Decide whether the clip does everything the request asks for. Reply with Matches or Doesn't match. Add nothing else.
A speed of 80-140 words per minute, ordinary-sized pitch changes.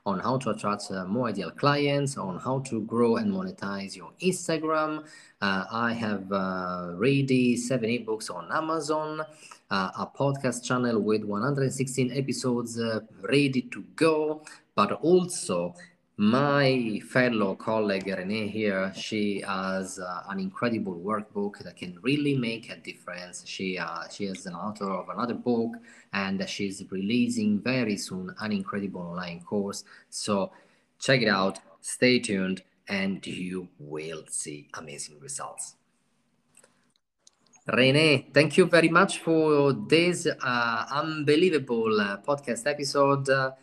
Doesn't match